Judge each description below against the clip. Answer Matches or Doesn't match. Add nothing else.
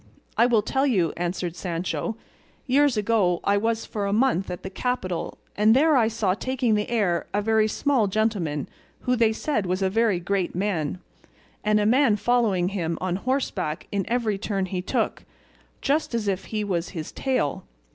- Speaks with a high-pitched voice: Matches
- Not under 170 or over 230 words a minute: Matches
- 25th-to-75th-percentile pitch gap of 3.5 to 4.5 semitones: Matches